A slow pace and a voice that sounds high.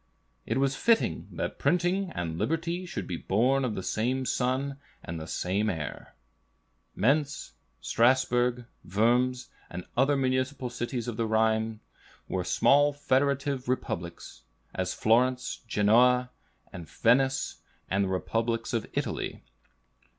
No: slow, 120 wpm; low, 125 Hz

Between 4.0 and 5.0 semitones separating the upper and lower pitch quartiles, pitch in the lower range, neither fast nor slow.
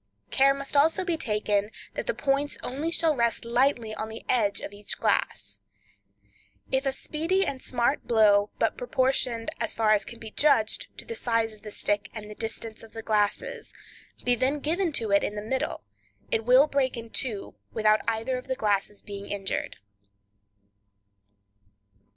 No: average, 4.3 semitones; high, 230 Hz; average, 175 wpm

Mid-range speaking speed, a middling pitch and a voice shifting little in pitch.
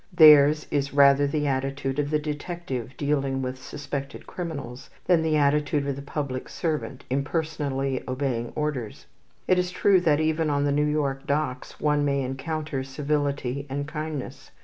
Yes: average, 155 wpm; medium, 145 Hz; narrow, 2.0 semitones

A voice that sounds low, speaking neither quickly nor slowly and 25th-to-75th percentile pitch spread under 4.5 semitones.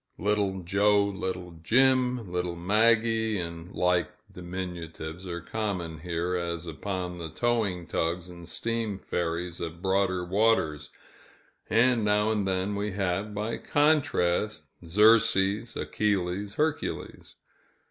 No: very low, 95 Hz; slow, 115 wpm; average, 3.6 semitones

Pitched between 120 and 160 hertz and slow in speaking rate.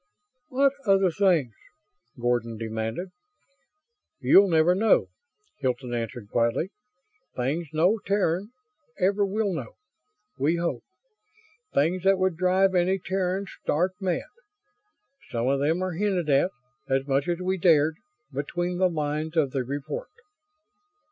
No: medium, 170 Hz; slow, 125 wpm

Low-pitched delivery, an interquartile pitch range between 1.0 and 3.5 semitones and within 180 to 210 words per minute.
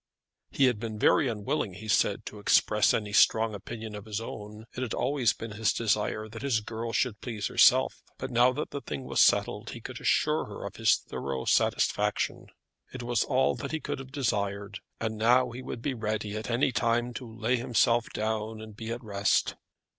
Yes: low, 110 Hz; narrow, 2.5 semitones; average, 200 wpm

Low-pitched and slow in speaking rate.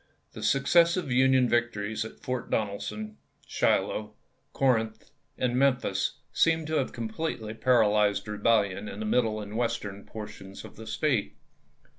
Yes: low, 115 Hz; slow, 130 wpm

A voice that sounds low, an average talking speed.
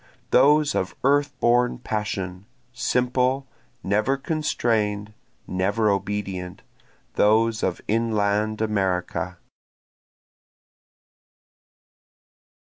No: low, 110 Hz; slow, 65 wpm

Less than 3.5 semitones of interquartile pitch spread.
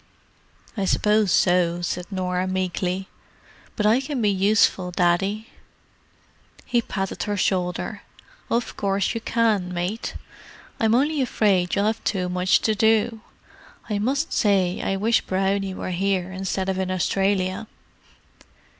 Yes: average, 2.8 semitones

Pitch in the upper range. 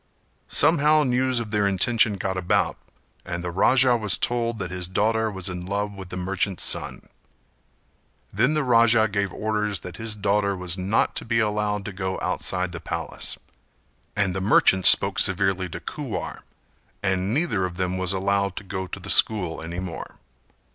No: low, 100 Hz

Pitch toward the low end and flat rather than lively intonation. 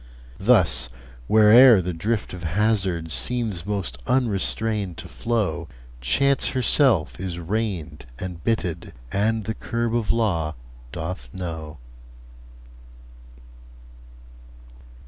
No: very low, 95 Hz; average, 5.2 semitones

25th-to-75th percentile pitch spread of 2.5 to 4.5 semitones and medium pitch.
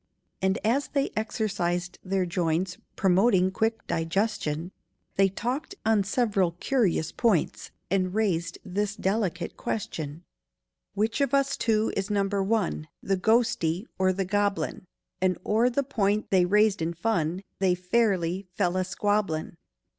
No: average, 3.5 semitones; high, 195 Hz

